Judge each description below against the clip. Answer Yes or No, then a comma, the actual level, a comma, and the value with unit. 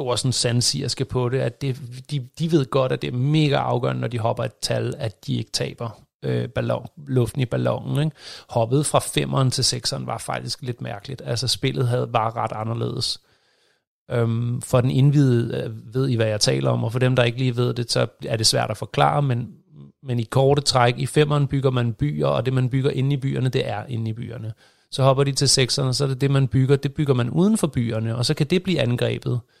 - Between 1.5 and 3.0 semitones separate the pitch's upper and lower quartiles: Yes, narrow, 2.6 semitones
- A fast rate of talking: Yes, fast, 235 wpm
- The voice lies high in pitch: No, low, 130 Hz